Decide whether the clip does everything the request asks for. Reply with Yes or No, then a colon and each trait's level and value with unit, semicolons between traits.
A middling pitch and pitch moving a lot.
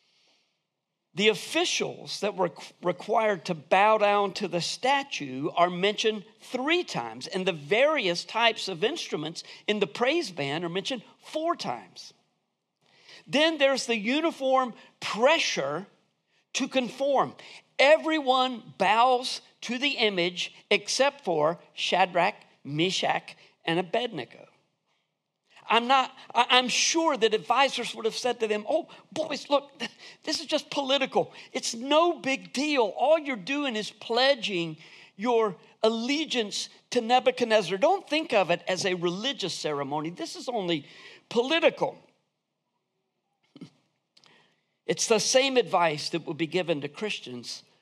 No: high, 225 Hz; wide, 6.6 semitones